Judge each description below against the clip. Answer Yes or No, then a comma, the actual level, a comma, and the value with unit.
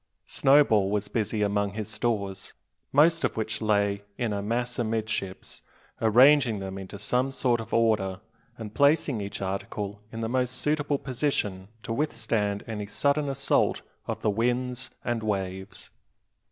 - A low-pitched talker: Yes, low, 110 Hz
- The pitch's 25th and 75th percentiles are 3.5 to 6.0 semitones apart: Yes, average, 3.8 semitones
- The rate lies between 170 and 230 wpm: No, average, 145 wpm